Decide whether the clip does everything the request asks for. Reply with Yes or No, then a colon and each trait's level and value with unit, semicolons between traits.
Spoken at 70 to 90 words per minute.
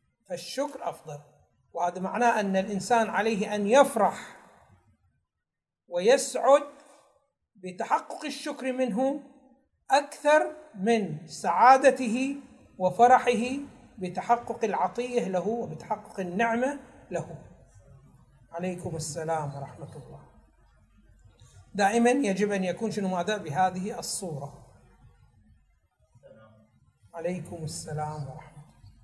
Yes: average, 80 wpm